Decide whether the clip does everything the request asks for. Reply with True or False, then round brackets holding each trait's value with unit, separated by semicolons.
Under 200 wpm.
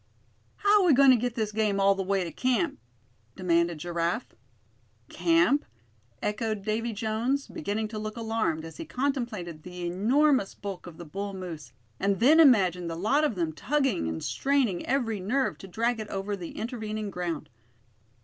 True (170 wpm)